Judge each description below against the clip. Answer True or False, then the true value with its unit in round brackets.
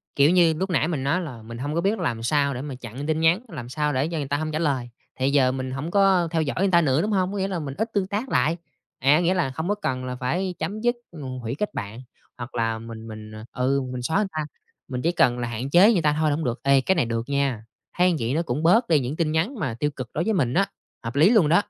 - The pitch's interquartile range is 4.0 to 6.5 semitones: True (5.3 semitones)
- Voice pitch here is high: False (150 Hz)